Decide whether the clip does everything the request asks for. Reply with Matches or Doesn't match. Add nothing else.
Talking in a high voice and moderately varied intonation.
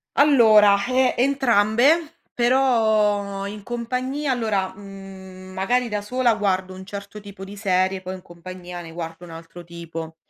Matches